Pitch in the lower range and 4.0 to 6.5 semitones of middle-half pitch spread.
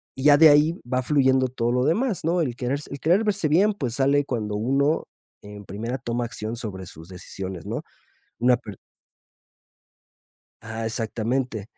Yes: low, 125 Hz; average, 4.7 semitones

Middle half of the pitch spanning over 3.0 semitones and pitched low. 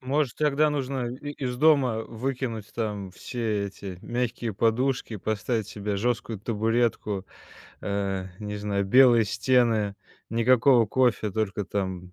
Yes: average, 3.6 semitones; low, 115 Hz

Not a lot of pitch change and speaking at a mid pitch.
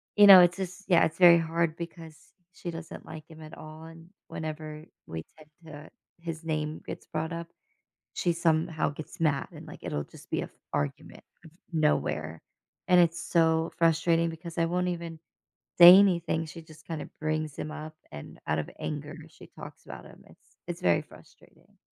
Yes: narrow, 1.6 semitones; medium, 160 Hz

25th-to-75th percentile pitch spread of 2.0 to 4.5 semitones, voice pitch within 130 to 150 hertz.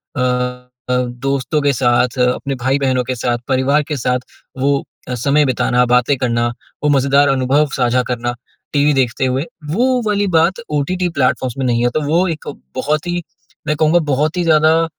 Yes: average, 3.3 semitones; low, 135 Hz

